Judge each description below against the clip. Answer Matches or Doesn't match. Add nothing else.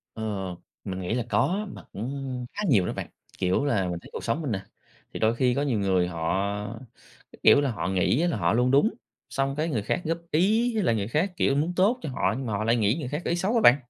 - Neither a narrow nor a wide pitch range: Doesn't match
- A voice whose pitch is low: Matches